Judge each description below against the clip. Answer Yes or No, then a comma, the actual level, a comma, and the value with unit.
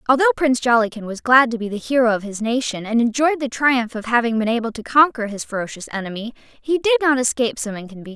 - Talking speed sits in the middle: No, fast, 230 wpm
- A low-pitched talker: No, high, 245 Hz